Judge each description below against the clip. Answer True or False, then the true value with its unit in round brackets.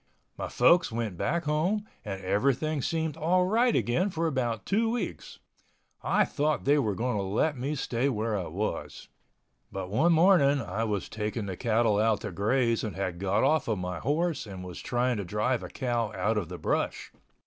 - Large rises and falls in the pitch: True (6.8 semitones)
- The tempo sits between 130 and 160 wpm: False (190 wpm)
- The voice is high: False (120 Hz)